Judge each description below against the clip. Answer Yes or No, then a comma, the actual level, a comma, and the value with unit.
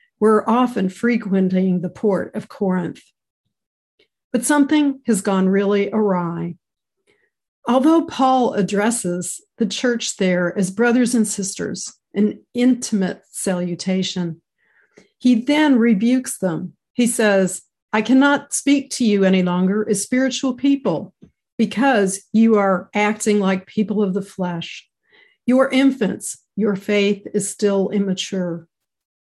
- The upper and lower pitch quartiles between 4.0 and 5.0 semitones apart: Yes, average, 4.7 semitones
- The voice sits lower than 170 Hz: No, high, 210 Hz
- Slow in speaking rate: Yes, slow, 120 wpm